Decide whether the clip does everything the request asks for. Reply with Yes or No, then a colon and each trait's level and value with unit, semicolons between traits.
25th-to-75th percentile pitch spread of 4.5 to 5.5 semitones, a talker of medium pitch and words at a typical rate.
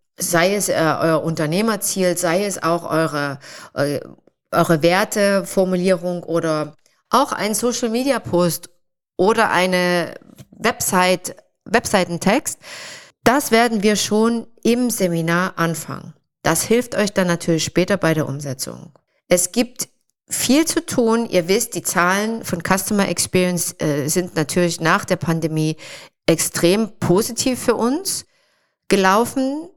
No: average, 4.8 semitones; medium, 180 Hz; slow, 115 wpm